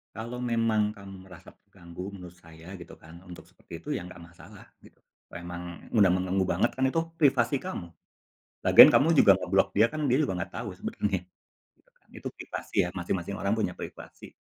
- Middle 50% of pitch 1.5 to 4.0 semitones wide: No, average, 4.7 semitones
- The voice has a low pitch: Yes, very low, 95 Hz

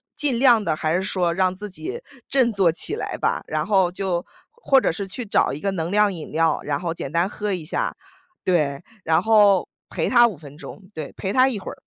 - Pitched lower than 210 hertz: Yes, high, 190 Hz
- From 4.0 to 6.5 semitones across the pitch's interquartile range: Yes, average, 4.5 semitones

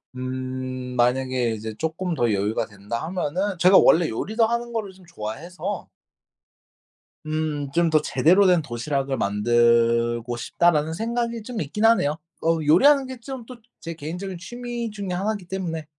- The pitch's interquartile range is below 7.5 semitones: No, wide, 7.9 semitones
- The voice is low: No, medium, 160 Hz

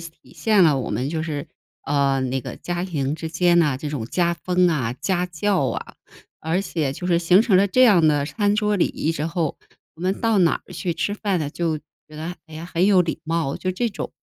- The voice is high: No, medium, 170 Hz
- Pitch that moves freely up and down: No, average, 3.5 semitones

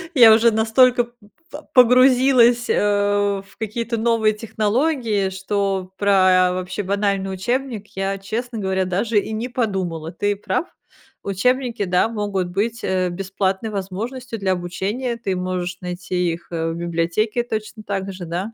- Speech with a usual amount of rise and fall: Yes, average, 3.6 semitones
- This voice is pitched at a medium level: No, high, 205 Hz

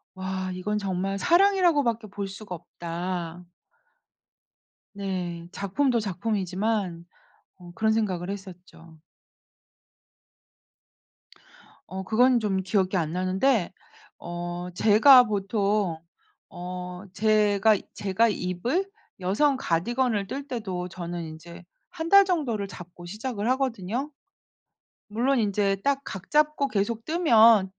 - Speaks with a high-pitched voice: Yes, high, 200 Hz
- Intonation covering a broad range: No, average, 4.4 semitones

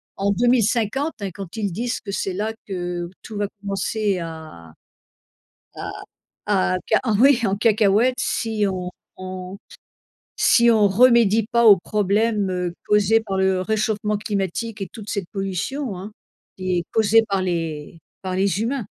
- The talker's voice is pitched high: Yes, high, 200 Hz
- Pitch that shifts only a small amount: No, average, 3.1 semitones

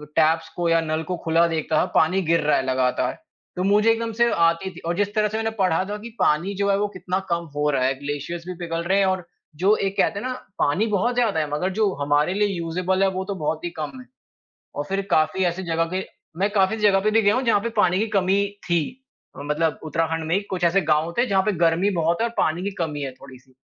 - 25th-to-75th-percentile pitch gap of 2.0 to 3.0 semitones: No, average, 3.8 semitones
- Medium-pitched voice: Yes, medium, 175 Hz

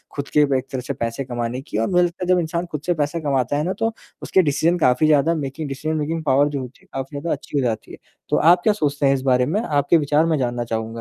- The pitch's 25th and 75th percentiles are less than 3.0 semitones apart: No, average, 3.9 semitones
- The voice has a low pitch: No, medium, 145 Hz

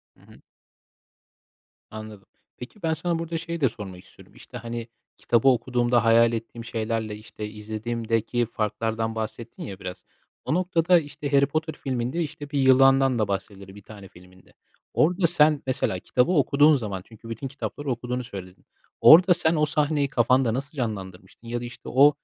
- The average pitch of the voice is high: No, low, 120 Hz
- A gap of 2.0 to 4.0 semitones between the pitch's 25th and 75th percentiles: No, average, 4.9 semitones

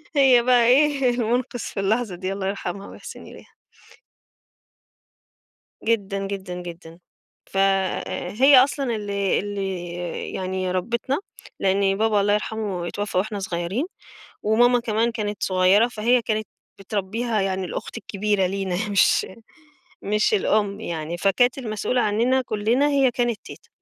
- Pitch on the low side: No, high, 205 Hz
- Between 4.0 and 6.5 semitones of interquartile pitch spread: No, average, 3.5 semitones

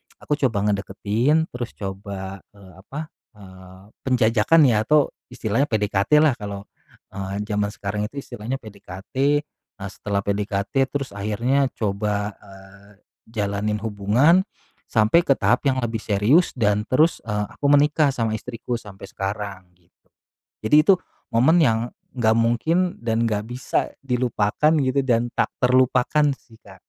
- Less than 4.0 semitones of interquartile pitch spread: No, average, 4.4 semitones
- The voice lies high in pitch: No, low, 110 Hz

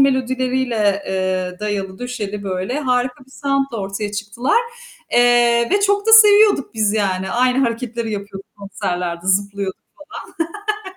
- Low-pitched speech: No, high, 230 Hz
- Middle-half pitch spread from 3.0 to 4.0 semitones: No, average, 4.7 semitones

